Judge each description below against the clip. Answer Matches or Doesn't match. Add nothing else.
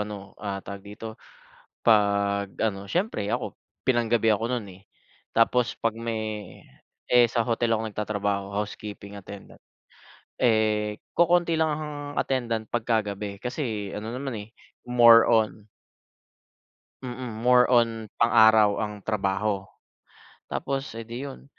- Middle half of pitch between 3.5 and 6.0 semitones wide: Doesn't match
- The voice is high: Doesn't match